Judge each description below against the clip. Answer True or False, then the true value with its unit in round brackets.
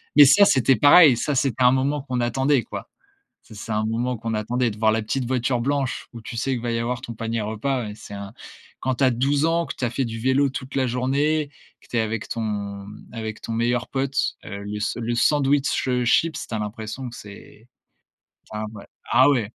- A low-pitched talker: True (120 Hz)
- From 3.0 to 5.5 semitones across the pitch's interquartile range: True (3.3 semitones)